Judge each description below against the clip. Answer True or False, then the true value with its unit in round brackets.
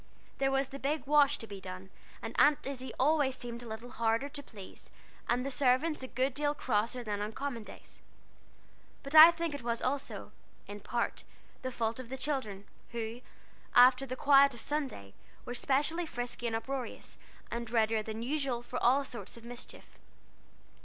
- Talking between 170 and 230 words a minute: True (180 wpm)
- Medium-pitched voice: False (250 Hz)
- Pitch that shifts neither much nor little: True (3.3 semitones)